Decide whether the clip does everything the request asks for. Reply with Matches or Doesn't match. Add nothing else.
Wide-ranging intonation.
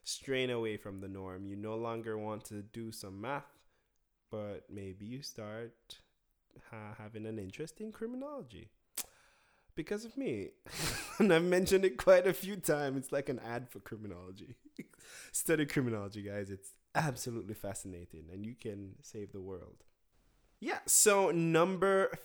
Matches